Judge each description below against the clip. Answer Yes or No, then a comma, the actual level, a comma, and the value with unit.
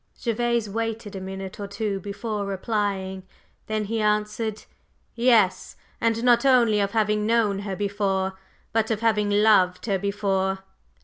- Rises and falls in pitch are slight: Yes, narrow, 2.3 semitones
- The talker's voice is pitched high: Yes, high, 210 Hz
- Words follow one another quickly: No, average, 140 wpm